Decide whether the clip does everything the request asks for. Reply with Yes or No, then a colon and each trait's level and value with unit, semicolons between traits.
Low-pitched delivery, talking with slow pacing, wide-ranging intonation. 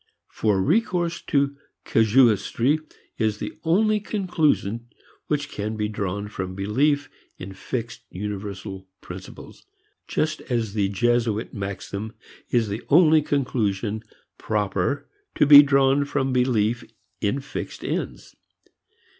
Yes: low, 115 Hz; slow, 115 wpm; wide, 5.7 semitones